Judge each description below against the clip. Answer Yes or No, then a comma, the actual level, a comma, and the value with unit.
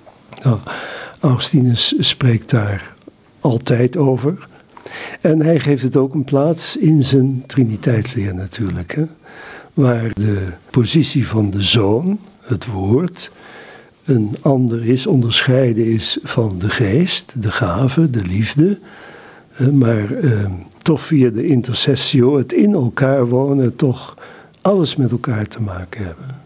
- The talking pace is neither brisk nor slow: No, slow, 125 wpm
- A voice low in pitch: Yes, low, 130 Hz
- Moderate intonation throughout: Yes, average, 4.4 semitones